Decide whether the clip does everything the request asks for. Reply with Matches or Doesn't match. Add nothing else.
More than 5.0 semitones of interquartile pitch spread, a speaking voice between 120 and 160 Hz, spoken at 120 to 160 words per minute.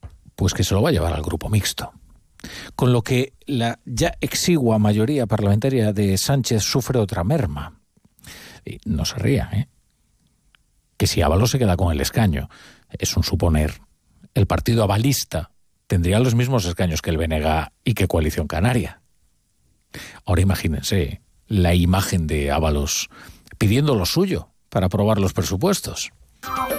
Doesn't match